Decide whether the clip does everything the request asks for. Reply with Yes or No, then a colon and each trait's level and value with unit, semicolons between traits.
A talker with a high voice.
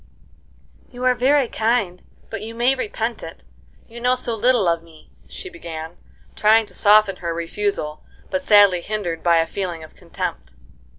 Yes: high, 210 Hz